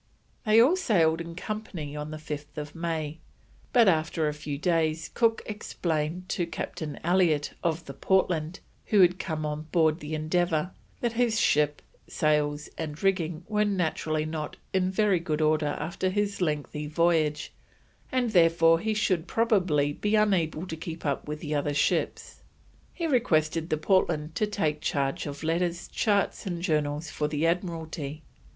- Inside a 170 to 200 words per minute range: No, average, 155 wpm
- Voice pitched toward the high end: No, medium, 165 Hz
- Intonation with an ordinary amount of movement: Yes, average, 3.6 semitones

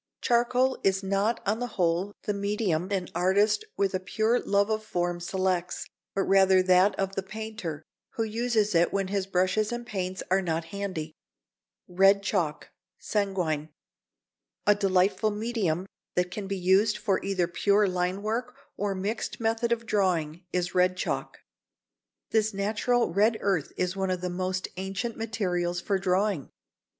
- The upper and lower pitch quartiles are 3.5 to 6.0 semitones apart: No, average, 2.7 semitones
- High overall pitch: Yes, high, 195 Hz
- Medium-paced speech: Yes, average, 160 wpm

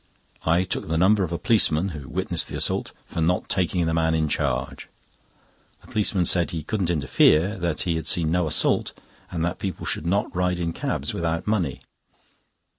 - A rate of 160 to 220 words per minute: Yes, average, 190 wpm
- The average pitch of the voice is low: Yes, very low, 85 Hz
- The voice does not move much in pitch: Yes, narrow, 2.2 semitones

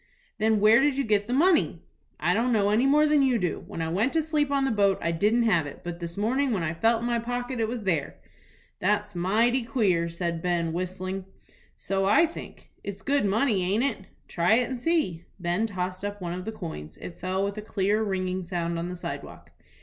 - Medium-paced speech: No, fast, 225 wpm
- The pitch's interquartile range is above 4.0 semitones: Yes, average, 5.0 semitones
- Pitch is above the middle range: Yes, high, 205 Hz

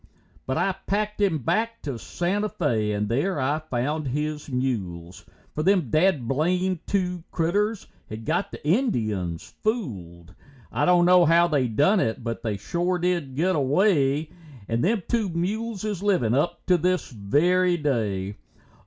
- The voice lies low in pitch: No, medium, 155 Hz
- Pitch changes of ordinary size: No, wide, 7.4 semitones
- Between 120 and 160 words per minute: Yes, average, 155 wpm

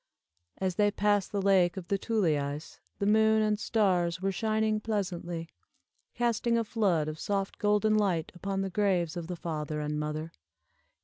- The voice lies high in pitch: Yes, high, 195 Hz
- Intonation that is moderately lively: Yes, average, 3.9 semitones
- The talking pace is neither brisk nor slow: Yes, average, 165 wpm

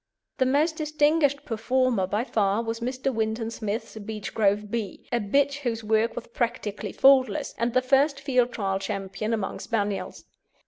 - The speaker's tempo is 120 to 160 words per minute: Yes, average, 150 wpm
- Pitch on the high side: Yes, high, 230 Hz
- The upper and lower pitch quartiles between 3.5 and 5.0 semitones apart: Yes, average, 3.8 semitones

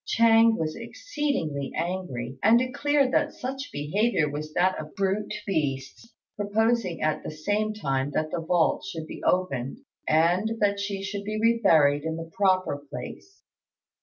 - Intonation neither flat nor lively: No, wide, 6.4 semitones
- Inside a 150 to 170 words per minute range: Yes, average, 155 wpm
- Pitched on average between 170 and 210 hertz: Yes, high, 190 Hz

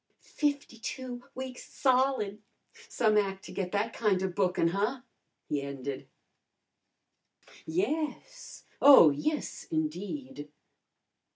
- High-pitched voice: Yes, high, 210 Hz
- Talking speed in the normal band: No, slow, 95 wpm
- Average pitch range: No, wide, 6.5 semitones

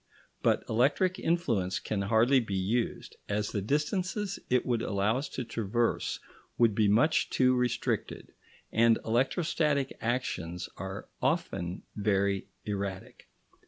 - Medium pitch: No, low, 115 Hz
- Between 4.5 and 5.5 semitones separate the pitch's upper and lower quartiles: Yes, average, 4.9 semitones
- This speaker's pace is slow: Yes, slow, 125 wpm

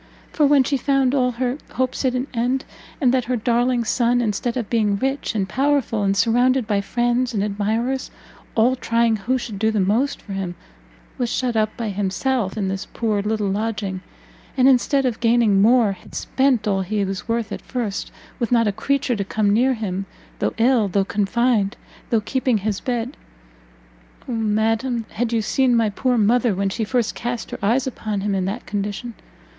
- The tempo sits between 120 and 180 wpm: No, average, 190 wpm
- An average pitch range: Yes, average, 3.5 semitones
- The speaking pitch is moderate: No, high, 230 Hz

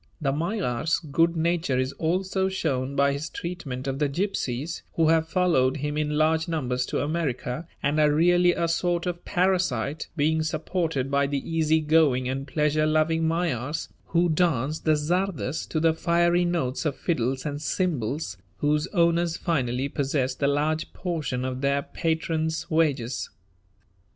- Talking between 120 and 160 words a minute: Yes, average, 155 wpm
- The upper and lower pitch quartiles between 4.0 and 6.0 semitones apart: No, average, 3.4 semitones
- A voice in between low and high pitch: Yes, medium, 155 Hz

